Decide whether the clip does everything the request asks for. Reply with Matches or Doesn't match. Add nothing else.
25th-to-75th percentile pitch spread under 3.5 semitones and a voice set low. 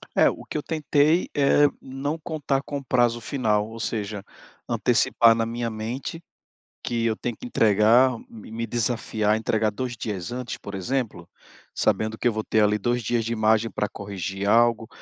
Matches